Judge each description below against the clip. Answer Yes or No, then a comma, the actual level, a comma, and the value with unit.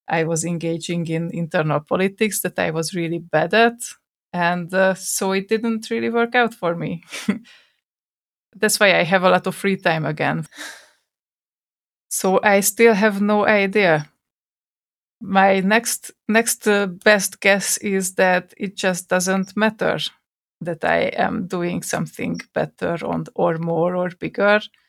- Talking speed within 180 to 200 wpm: No, average, 145 wpm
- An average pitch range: Yes, average, 3.4 semitones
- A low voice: No, high, 190 Hz